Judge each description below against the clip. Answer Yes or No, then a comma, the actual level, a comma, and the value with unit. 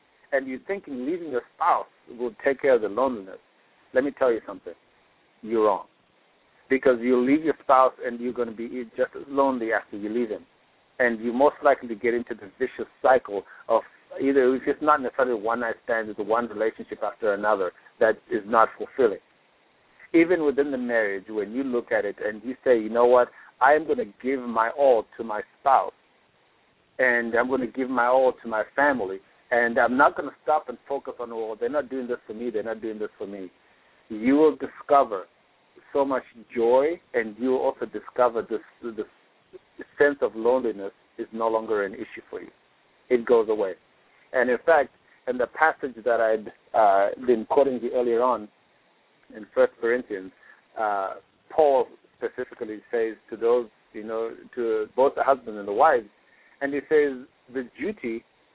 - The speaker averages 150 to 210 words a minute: Yes, average, 190 wpm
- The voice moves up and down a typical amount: Yes, average, 4.0 semitones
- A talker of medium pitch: No, low, 125 Hz